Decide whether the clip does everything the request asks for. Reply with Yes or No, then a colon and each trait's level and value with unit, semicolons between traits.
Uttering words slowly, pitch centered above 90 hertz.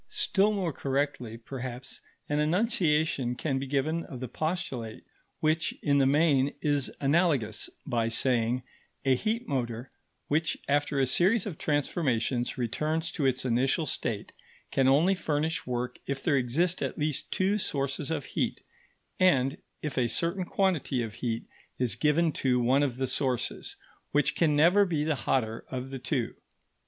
No: average, 155 wpm; medium, 140 Hz